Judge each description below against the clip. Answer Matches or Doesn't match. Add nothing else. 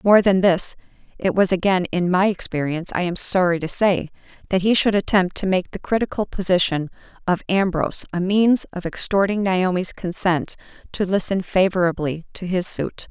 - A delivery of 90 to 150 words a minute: Doesn't match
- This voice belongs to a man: Doesn't match